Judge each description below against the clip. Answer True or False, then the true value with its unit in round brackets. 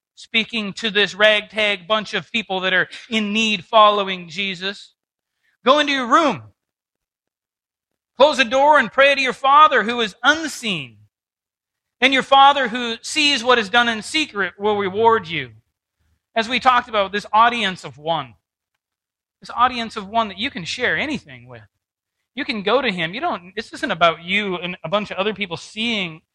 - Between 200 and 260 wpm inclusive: False (175 wpm)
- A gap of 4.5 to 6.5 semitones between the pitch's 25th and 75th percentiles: True (5.4 semitones)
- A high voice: True (215 Hz)